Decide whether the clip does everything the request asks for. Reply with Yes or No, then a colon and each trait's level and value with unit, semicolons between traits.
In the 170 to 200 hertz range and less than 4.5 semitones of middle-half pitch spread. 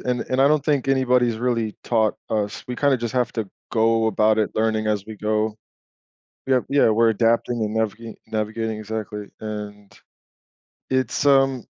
No: low, 110 Hz; narrow, 2.6 semitones